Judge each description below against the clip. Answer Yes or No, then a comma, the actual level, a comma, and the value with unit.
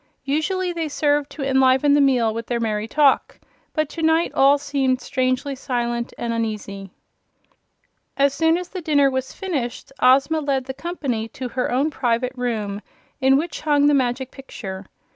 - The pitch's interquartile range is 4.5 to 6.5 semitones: No, average, 3.3 semitones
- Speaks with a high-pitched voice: Yes, very high, 265 Hz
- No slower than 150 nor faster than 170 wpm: Yes, average, 165 wpm